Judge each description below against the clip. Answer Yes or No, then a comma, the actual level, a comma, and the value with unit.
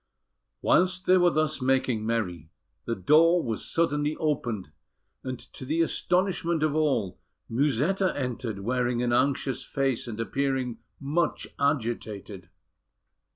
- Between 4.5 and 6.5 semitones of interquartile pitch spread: Yes, average, 5.1 semitones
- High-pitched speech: No, low, 135 Hz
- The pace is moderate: No, slow, 120 wpm